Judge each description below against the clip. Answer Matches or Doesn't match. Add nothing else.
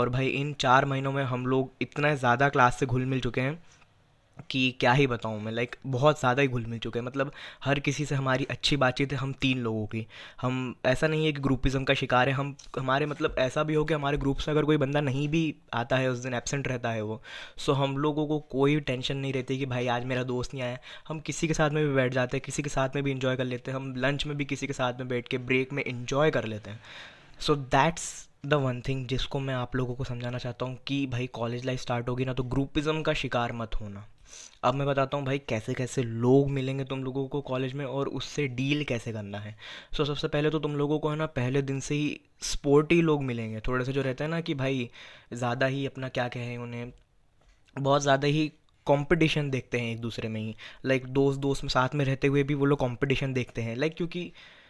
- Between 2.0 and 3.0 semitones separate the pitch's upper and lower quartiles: Matches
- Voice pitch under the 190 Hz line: Matches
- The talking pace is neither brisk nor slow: Doesn't match